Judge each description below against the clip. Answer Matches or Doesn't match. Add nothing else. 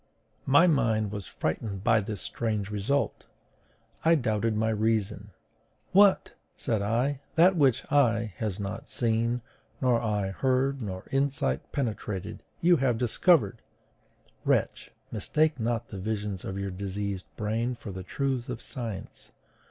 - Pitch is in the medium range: Doesn't match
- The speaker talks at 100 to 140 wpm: Matches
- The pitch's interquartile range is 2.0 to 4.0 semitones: Doesn't match